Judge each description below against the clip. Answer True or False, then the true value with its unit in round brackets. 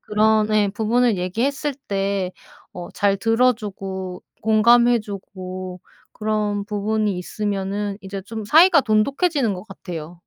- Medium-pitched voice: False (210 Hz)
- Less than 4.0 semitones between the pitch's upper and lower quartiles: True (2.6 semitones)